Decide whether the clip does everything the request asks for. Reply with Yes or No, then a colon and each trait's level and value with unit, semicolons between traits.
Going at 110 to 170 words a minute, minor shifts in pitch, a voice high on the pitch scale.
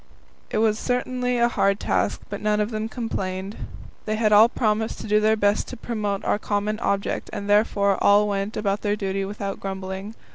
No: average, 190 wpm; narrow, 1.6 semitones; high, 210 Hz